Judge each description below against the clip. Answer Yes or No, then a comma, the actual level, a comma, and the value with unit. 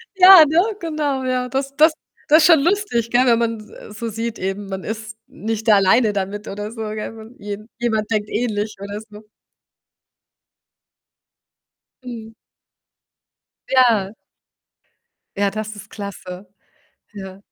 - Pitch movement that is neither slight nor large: Yes, average, 3.5 semitones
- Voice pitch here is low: No, high, 220 Hz